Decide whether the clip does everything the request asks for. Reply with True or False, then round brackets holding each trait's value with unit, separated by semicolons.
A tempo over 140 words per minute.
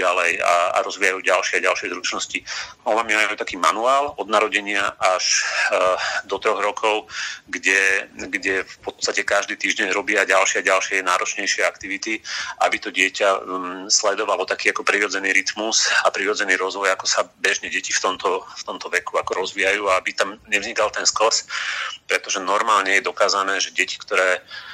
True (160 wpm)